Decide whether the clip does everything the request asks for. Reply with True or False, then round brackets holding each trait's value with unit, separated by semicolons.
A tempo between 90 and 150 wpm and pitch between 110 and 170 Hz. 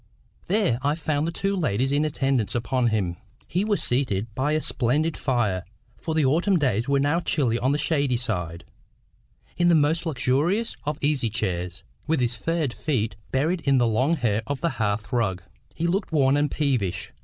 False (185 wpm; 135 Hz)